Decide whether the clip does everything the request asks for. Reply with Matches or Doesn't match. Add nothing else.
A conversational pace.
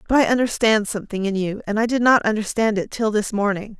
Doesn't match